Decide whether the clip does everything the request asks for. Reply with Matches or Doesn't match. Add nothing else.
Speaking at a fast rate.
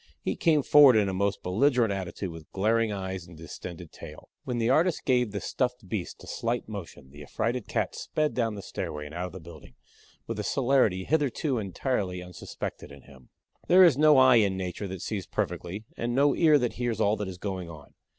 Matches